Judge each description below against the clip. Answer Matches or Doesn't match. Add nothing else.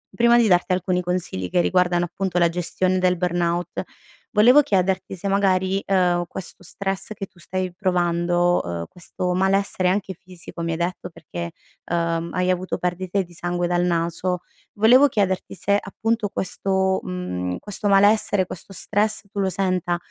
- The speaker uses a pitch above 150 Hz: Matches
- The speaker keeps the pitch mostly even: Matches